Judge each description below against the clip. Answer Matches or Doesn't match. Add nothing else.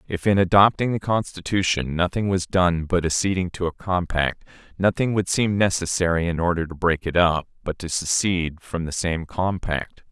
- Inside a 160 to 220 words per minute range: Matches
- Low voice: Matches